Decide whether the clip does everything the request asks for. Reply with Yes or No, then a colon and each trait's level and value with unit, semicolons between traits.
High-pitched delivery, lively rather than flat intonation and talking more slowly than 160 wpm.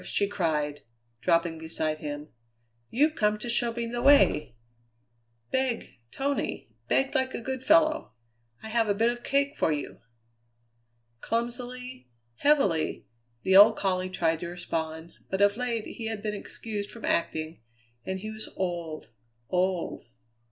Yes: high, 210 Hz; wide, 6.3 semitones; average, 145 wpm